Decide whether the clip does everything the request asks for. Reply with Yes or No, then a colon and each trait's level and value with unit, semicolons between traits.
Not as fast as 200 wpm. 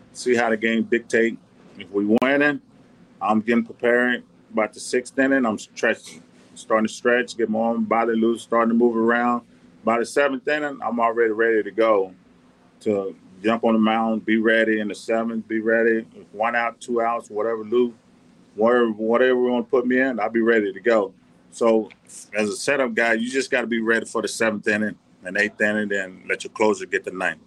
No: fast, 205 wpm